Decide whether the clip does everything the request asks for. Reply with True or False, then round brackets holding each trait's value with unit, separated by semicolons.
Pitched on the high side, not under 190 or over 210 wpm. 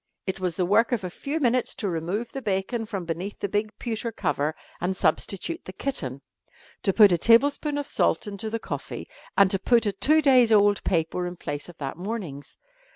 True (200 Hz; 205 wpm)